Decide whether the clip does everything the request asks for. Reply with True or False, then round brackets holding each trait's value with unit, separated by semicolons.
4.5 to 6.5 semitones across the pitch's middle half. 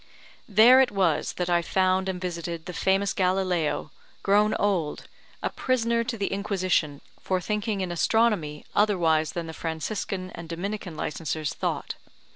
False (3.5 semitones)